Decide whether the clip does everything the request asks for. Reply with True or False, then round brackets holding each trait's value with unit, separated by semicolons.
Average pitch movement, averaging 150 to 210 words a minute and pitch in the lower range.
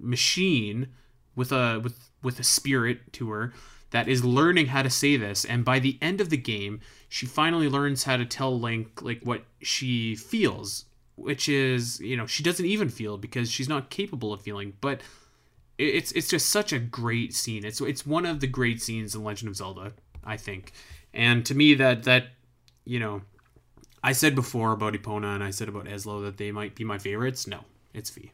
True (4.0 semitones; 200 wpm; 120 Hz)